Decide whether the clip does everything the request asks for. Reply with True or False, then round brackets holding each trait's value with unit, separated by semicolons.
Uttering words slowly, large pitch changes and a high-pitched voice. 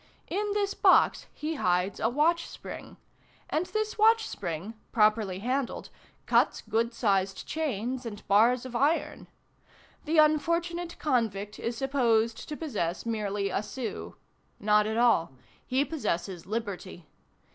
True (130 wpm; 6.9 semitones; 235 Hz)